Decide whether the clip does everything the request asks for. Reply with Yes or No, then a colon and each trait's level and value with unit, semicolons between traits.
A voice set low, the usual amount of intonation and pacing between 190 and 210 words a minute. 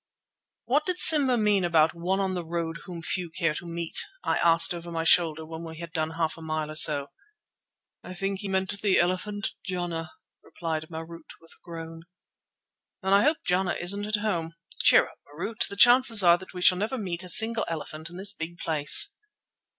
No: medium, 175 Hz; average, 3.4 semitones; average, 195 wpm